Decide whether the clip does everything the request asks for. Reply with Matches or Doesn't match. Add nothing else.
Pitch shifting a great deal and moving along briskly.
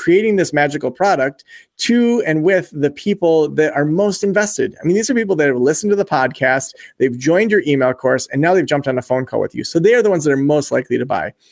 Matches